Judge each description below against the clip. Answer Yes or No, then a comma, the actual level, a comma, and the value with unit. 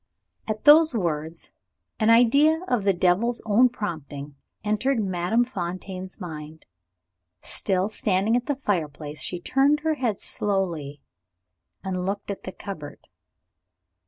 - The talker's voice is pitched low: No, high, 195 Hz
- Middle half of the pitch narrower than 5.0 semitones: No, wide, 5.5 semitones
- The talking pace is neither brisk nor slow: No, slow, 125 wpm